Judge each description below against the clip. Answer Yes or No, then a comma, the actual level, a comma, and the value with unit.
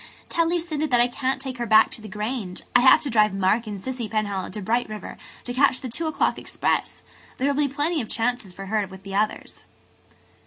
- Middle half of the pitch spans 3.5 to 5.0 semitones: Yes, average, 4.1 semitones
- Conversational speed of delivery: No, fast, 225 wpm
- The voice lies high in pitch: Yes, high, 235 Hz